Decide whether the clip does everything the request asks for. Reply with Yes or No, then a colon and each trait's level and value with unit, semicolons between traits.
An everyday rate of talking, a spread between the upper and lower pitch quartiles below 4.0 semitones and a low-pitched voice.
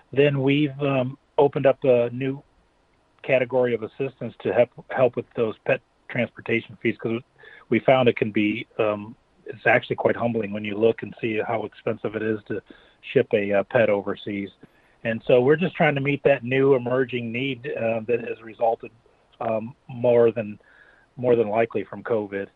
Yes: average, 180 wpm; average, 3.3 semitones; low, 120 Hz